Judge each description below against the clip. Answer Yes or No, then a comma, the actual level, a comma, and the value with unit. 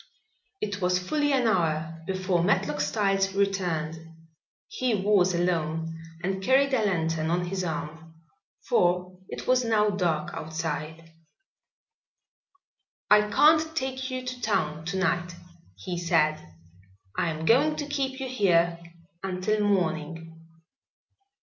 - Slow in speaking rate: Yes, slow, 125 wpm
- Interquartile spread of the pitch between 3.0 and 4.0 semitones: No, average, 4.6 semitones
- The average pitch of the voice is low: No, medium, 180 Hz